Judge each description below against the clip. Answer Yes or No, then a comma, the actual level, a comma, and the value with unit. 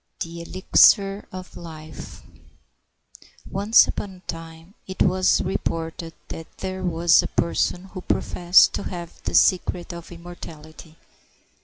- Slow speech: Yes, slow, 125 wpm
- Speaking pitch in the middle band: Yes, medium, 175 Hz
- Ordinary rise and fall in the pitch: No, narrow, 2.2 semitones